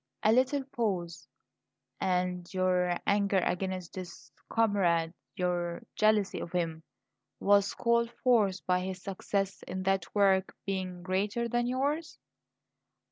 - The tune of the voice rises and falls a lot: No, average, 3.0 semitones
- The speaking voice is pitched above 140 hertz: Yes, high, 190 Hz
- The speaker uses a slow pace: Yes, slow, 120 wpm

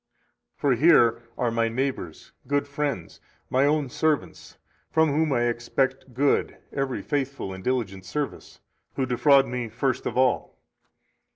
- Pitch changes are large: No, average, 3.1 semitones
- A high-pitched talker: No, low, 130 Hz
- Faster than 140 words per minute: No, slow, 135 wpm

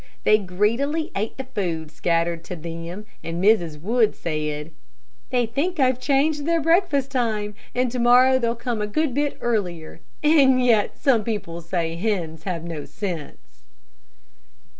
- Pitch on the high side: Yes, high, 215 Hz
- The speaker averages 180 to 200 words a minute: No, average, 150 wpm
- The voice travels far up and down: Yes, wide, 7.4 semitones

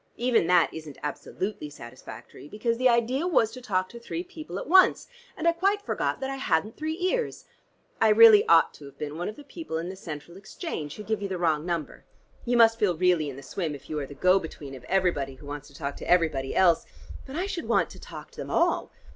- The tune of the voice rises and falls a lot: Yes, wide, 7.9 semitones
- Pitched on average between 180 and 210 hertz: Yes, medium, 185 Hz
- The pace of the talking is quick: Yes, fast, 240 wpm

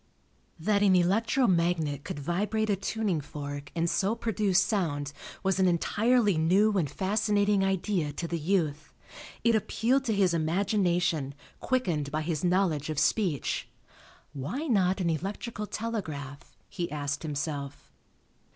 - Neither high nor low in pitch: Yes, medium, 180 Hz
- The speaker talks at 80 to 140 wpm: Yes, slow, 135 wpm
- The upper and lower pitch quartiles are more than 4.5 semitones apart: Yes, average, 5.2 semitones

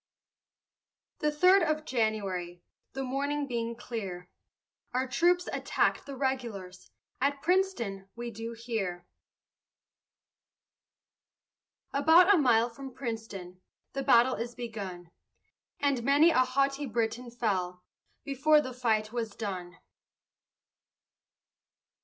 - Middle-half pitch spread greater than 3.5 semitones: Yes, average, 4.6 semitones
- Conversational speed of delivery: No, slow, 105 wpm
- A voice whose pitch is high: Yes, high, 240 Hz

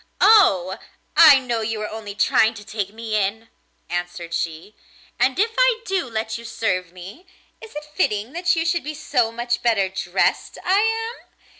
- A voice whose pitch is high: Yes, high, 225 Hz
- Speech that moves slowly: No, average, 175 wpm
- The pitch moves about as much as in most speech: No, wide, 8.7 semitones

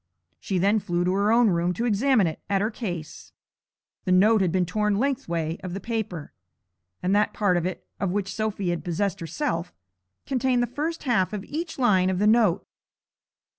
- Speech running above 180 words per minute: Yes, average, 190 wpm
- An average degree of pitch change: Yes, average, 4.1 semitones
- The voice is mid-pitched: No, high, 200 Hz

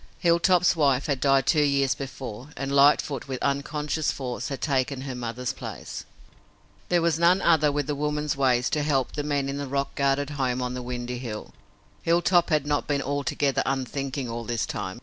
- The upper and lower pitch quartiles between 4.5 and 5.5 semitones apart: No, narrow, 2.5 semitones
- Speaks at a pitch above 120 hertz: Yes, medium, 140 Hz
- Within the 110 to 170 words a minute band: No, average, 185 wpm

